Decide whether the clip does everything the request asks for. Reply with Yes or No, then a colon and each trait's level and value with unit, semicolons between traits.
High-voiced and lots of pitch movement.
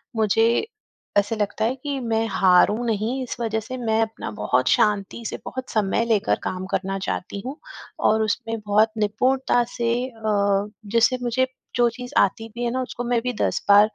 No: high, 225 Hz; average, 2.8 semitones